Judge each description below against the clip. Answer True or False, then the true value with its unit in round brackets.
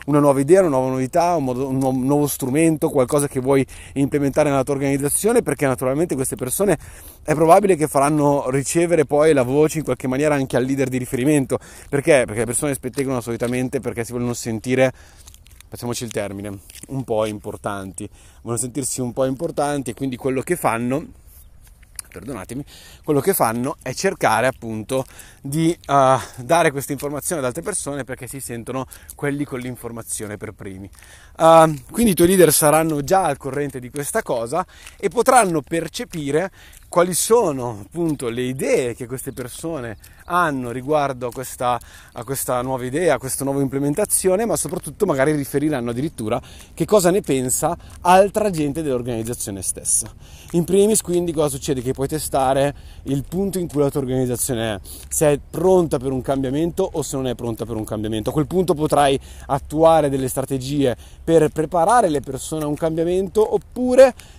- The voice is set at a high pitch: False (140 Hz)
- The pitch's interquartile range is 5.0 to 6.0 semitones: False (4.2 semitones)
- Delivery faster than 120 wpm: True (165 wpm)